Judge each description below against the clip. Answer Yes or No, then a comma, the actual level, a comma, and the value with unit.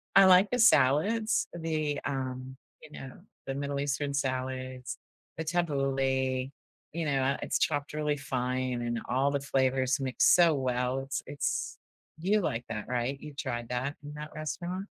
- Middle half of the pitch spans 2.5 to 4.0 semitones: Yes, average, 2.9 semitones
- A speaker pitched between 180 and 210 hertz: No, medium, 140 Hz